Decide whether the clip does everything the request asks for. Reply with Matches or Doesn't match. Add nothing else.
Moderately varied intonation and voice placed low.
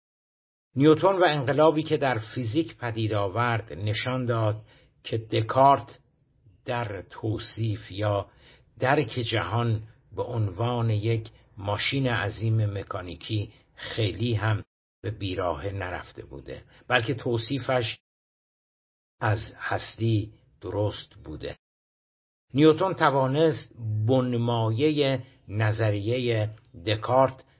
Matches